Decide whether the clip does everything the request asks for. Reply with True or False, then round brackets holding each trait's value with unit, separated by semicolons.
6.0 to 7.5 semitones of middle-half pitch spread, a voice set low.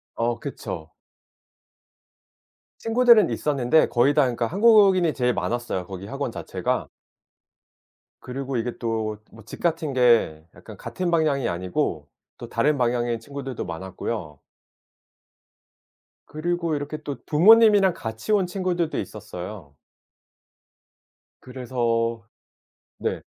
True (6.6 semitones; 130 Hz)